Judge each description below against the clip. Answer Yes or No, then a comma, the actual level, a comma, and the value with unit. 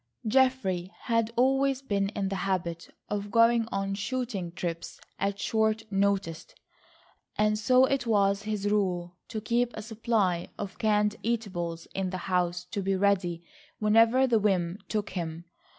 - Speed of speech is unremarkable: Yes, average, 150 wpm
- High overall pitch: Yes, high, 205 Hz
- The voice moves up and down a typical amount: Yes, average, 3.5 semitones